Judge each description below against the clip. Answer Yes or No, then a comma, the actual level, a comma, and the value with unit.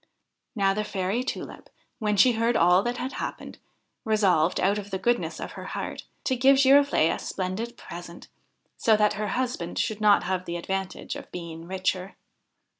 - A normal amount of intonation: Yes, average, 4.4 semitones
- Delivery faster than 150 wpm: Yes, average, 180 wpm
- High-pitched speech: Yes, high, 205 Hz